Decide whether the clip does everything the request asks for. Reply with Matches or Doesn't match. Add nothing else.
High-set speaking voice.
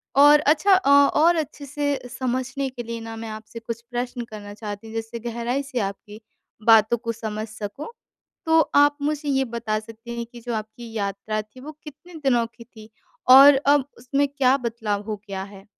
Matches